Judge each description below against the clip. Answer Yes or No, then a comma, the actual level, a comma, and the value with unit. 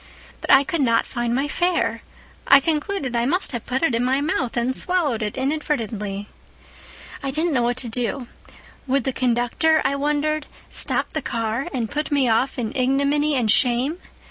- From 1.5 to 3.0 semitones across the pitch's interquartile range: No, average, 3.7 semitones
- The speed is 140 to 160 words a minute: No, average, 180 wpm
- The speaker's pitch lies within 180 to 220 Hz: No, very high, 265 Hz